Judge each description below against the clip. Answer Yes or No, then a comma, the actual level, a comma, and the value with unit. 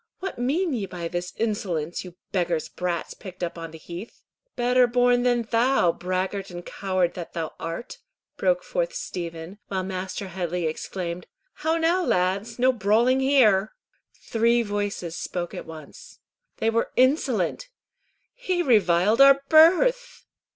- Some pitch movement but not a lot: No, wide, 6.5 semitones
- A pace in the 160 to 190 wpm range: No, average, 145 wpm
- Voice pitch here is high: Yes, high, 205 Hz